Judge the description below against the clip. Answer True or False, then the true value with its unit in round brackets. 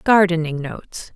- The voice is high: False (175 Hz)